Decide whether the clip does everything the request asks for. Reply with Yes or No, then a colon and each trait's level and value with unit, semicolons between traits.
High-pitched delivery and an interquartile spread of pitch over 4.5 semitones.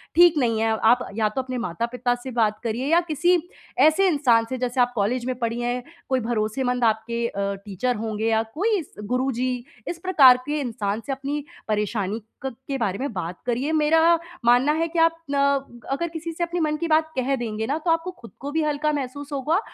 Yes: very high, 255 Hz; average, 5.1 semitones